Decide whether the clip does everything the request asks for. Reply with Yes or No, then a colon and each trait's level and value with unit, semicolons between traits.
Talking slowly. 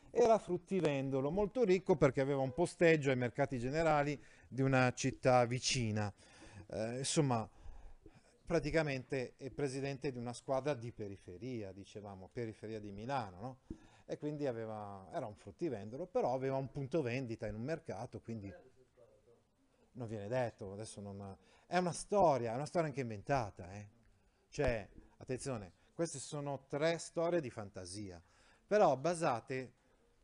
No: average, 140 wpm